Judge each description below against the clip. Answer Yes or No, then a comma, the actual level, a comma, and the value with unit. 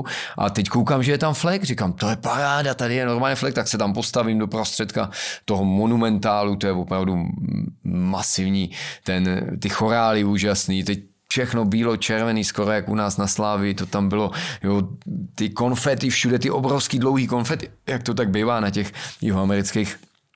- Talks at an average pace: No, fast, 175 wpm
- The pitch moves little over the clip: No, average, 3.8 semitones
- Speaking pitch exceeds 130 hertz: No, low, 110 Hz